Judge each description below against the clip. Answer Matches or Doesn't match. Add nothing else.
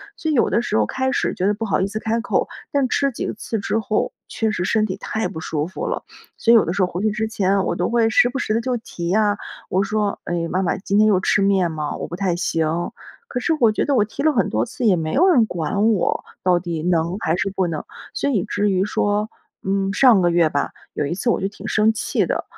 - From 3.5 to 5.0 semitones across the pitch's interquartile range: Matches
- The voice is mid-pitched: Doesn't match